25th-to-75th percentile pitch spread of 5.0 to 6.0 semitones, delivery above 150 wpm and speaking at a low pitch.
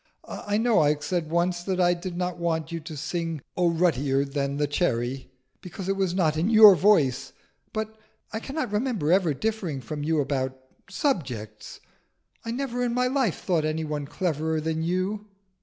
No: wide, 5.4 semitones; average, 175 wpm; medium, 170 Hz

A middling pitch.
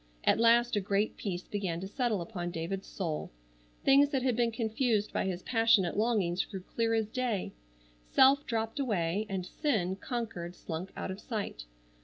No: high, 210 Hz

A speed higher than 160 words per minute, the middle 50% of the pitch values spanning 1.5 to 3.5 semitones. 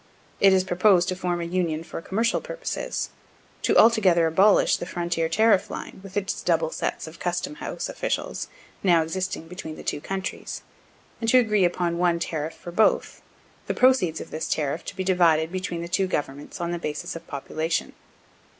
Yes: average, 180 wpm; average, 2.8 semitones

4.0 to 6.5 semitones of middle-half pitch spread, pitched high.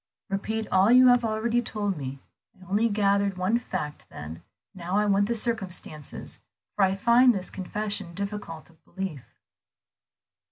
No: average, 3.0 semitones; high, 200 Hz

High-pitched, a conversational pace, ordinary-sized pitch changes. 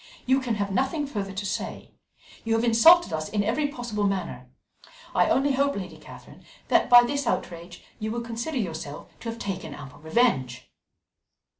No: high, 225 Hz; average, 170 wpm; wide, 5.7 semitones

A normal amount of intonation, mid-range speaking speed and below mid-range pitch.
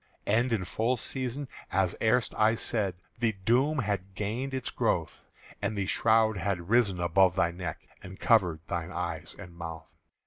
Yes: average, 4.6 semitones; average, 165 wpm; low, 100 Hz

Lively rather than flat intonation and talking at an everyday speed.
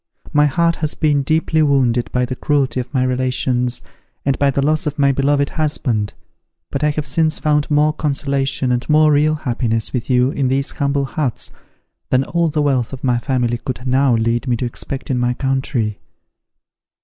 No: average, 2.9 semitones; average, 185 wpm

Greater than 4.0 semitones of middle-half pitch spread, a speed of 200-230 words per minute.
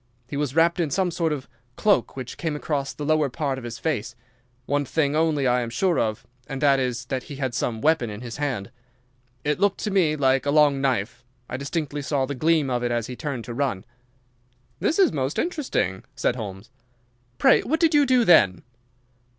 Yes: average, 4.5 semitones; fast, 205 wpm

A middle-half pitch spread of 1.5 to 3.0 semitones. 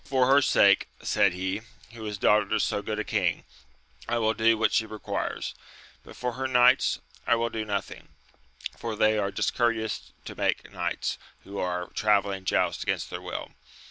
Yes: average, 2.7 semitones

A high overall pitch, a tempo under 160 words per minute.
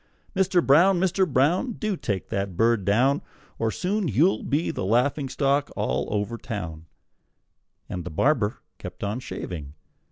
No: low, 130 Hz; average, 150 wpm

